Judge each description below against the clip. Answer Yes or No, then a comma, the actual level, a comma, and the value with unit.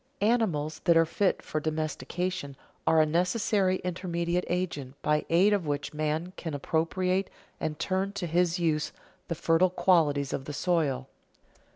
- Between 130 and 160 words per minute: Yes, average, 150 wpm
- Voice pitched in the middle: Yes, medium, 170 Hz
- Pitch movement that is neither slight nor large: Yes, average, 3.2 semitones